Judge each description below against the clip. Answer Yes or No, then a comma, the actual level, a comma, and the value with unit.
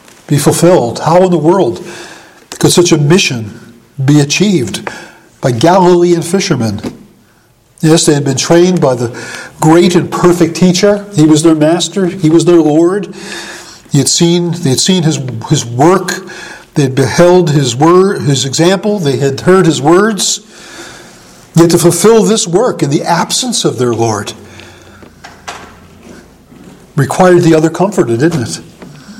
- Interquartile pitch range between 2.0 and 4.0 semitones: No, average, 4.7 semitones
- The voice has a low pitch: No, medium, 165 Hz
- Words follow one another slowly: No, average, 150 wpm